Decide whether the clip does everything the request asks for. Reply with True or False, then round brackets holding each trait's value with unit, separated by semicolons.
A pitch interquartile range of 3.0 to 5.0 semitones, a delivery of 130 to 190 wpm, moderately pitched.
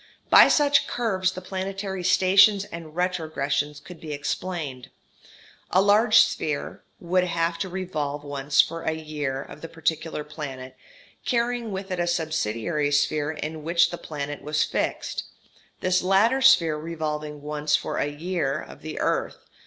True (3.9 semitones; 150 wpm; 165 Hz)